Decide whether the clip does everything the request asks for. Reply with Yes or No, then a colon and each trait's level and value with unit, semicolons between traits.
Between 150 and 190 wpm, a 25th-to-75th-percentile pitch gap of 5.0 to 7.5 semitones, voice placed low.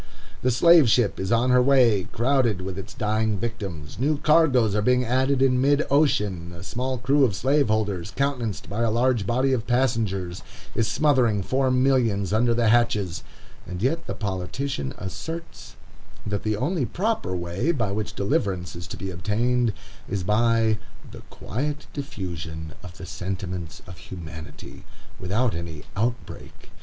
Yes: average, 155 wpm; average, 5.3 semitones; low, 115 Hz